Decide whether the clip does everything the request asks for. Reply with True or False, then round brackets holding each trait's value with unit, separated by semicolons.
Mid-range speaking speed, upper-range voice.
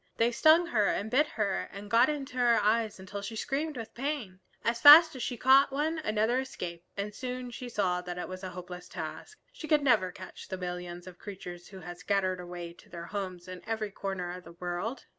False (215 wpm; 205 Hz)